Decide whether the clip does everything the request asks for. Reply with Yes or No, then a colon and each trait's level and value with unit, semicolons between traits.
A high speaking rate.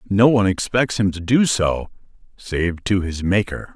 No: average, 160 wpm